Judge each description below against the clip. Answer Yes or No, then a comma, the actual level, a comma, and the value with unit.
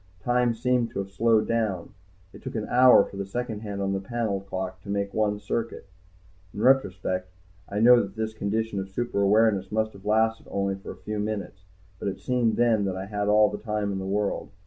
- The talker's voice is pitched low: Yes, low, 105 Hz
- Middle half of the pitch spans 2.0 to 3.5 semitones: Yes, narrow, 2.4 semitones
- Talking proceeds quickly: Yes, fast, 215 wpm